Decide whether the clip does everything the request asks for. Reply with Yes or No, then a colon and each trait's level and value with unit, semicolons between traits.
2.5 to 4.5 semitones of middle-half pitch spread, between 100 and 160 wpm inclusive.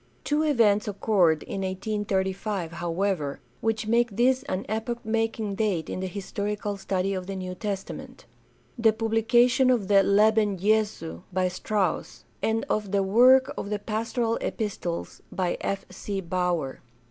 Yes: average, 2.9 semitones; average, 145 wpm